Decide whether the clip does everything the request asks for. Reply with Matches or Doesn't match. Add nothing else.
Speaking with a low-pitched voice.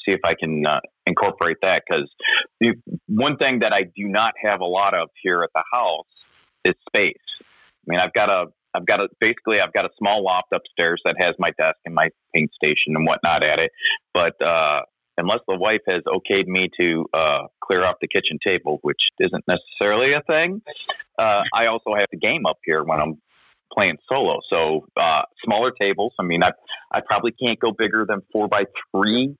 Matches